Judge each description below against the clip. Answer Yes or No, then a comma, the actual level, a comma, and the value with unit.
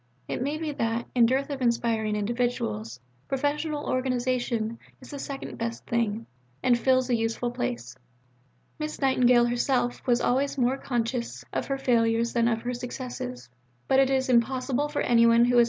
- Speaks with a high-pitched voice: Yes, high, 245 Hz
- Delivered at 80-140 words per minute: Yes, slow, 135 wpm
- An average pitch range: No, narrow, 2.3 semitones